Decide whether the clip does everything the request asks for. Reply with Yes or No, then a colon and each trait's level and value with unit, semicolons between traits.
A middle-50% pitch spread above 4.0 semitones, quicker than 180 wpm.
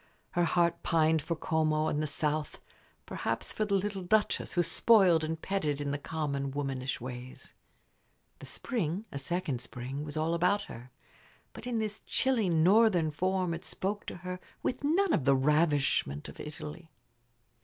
No: average, 4.7 semitones; average, 165 wpm